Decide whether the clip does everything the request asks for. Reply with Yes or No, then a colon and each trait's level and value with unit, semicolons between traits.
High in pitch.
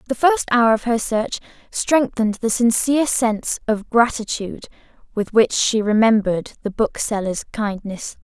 Yes: high, 225 Hz